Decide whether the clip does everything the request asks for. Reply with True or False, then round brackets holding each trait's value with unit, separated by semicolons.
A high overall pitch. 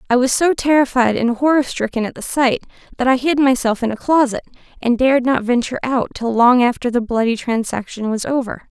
True (245 Hz)